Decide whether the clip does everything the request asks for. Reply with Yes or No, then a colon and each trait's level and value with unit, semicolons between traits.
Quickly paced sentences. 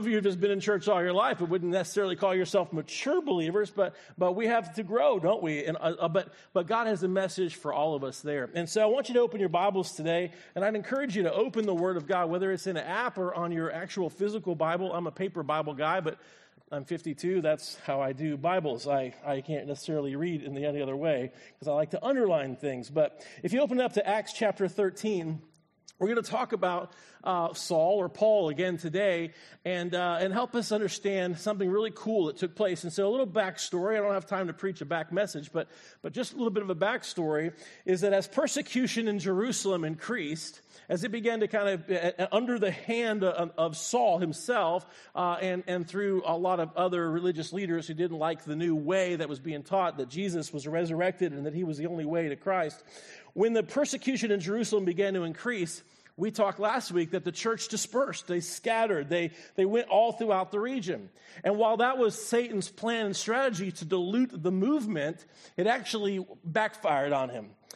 Yes: fast, 220 wpm